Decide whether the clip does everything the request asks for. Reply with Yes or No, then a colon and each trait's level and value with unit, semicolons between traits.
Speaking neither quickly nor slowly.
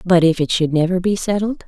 No: fast, 250 wpm